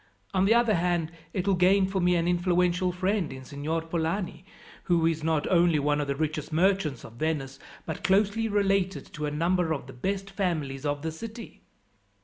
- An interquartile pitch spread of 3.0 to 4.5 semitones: Yes, average, 3.9 semitones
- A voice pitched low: No, medium, 175 Hz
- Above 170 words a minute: Yes, average, 190 wpm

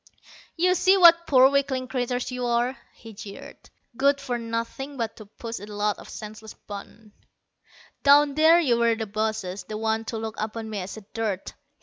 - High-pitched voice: Yes, high, 230 Hz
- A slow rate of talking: No, average, 180 wpm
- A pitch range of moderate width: Yes, average, 4.0 semitones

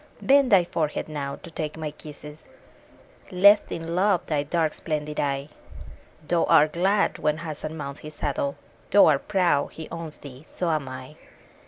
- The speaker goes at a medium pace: Yes, average, 175 wpm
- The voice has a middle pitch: Yes, medium, 155 Hz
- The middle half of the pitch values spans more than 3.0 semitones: No, average, 2.7 semitones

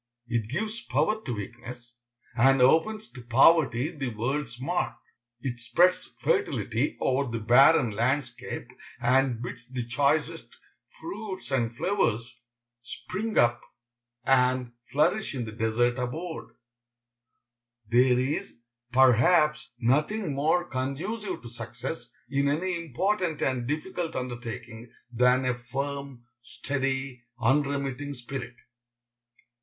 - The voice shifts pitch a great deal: No, average, 4.2 semitones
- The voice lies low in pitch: Yes, low, 130 Hz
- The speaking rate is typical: No, slow, 110 wpm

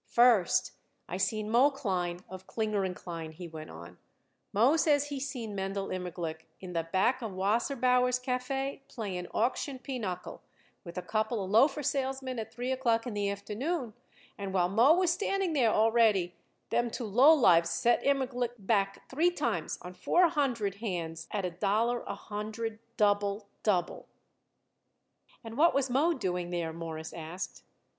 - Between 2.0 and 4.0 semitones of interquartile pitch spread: No, wide, 5.6 semitones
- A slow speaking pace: No, average, 160 wpm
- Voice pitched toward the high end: Yes, high, 220 Hz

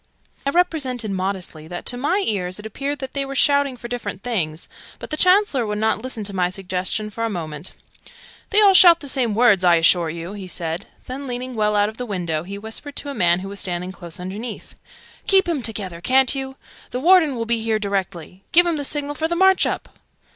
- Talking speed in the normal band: No, fast, 215 wpm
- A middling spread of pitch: No, wide, 6.9 semitones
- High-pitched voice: Yes, high, 220 Hz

